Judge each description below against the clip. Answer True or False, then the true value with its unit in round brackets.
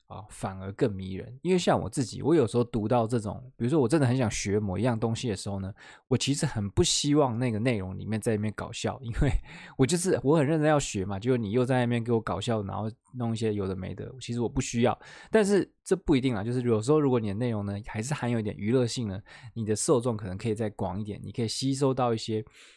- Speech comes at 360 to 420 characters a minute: True (375 characters per minute)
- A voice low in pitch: True (120 Hz)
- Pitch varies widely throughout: False (3.7 semitones)